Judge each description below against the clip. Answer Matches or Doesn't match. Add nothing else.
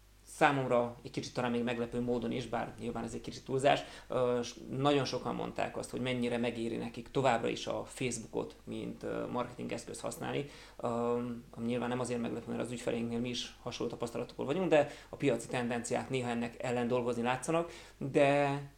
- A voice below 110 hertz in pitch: Doesn't match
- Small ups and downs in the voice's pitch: Matches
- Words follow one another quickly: Matches